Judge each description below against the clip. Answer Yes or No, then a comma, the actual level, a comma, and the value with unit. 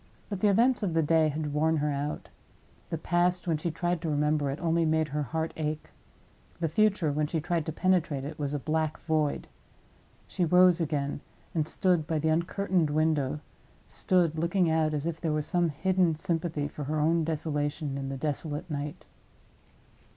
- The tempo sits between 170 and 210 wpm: Yes, average, 180 wpm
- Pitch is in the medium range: Yes, medium, 160 Hz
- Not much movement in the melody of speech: Yes, narrow, 2.2 semitones